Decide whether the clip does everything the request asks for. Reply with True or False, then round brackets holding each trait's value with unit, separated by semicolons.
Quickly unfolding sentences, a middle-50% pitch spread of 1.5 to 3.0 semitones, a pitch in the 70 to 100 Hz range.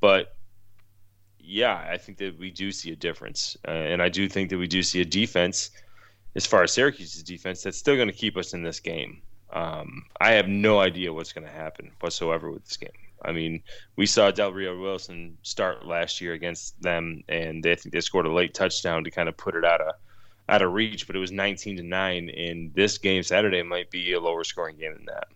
True (225 wpm; 2.7 semitones; 95 Hz)